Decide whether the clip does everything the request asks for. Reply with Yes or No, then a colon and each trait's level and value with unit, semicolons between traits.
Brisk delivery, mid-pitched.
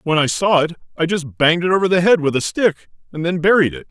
Yes: fast, 275 wpm; medium, 165 Hz